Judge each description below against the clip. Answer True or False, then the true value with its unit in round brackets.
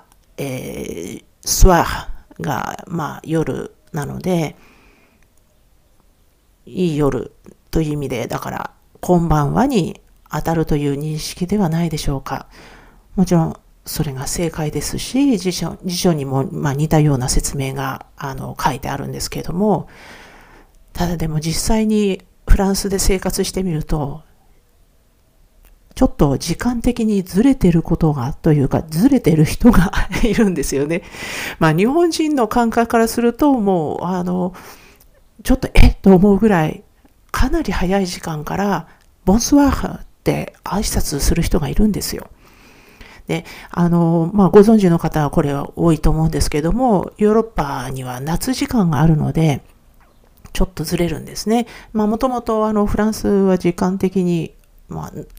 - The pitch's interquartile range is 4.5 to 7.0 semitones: True (5.3 semitones)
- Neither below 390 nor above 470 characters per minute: False (285 characters per minute)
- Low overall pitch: False (175 Hz)